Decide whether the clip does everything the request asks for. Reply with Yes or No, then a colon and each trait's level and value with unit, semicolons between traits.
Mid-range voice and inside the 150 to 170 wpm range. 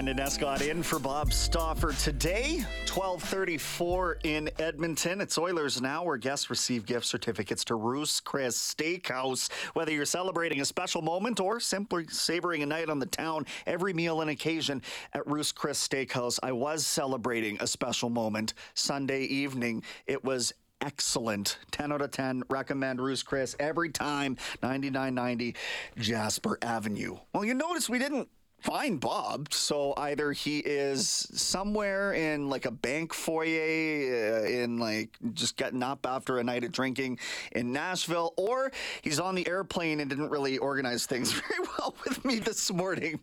Yes: medium, 145 Hz; average, 155 wpm